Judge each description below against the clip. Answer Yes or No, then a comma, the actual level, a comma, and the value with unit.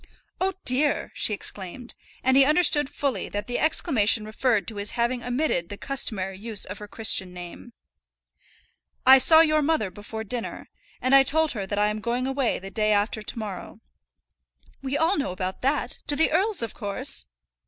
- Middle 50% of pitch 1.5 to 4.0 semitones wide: No, average, 5.2 semitones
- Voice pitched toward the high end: Yes, high, 240 Hz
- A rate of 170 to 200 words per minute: Yes, average, 180 wpm